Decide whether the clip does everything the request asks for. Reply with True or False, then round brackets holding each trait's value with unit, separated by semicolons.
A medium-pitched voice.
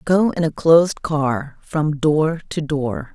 True (155 Hz)